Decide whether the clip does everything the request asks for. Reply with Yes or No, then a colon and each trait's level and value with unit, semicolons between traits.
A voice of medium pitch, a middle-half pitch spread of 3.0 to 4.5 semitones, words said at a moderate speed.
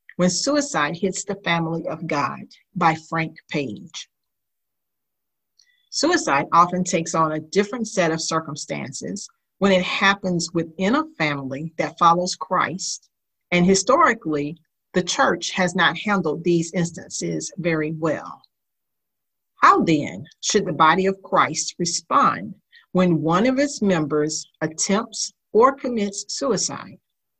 No: medium, 180 Hz; average, 3.7 semitones; slow, 125 wpm